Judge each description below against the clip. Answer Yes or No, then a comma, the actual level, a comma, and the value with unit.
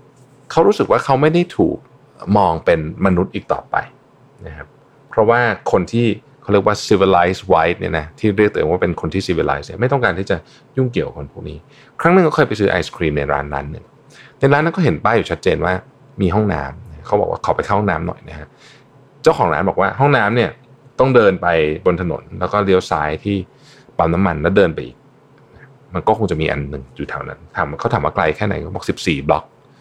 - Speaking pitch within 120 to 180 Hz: No, low, 105 Hz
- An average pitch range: No, wide, 7.8 semitones